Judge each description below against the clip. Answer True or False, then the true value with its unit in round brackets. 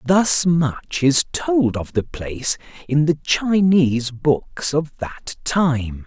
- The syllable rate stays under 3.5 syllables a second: True (3.1 syllables/s)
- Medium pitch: True (145 Hz)